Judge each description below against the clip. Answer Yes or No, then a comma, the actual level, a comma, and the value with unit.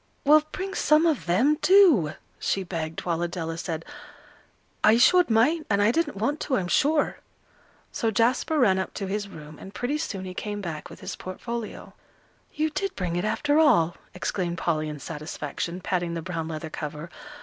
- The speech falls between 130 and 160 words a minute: No, average, 180 wpm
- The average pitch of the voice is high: Yes, high, 195 Hz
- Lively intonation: Yes, wide, 9.0 semitones